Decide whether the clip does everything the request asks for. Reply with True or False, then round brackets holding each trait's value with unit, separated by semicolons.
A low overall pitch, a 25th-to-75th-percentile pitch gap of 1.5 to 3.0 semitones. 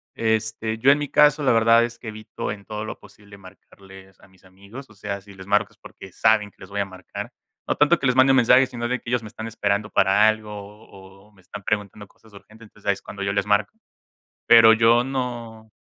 True (105 Hz; 2.7 semitones)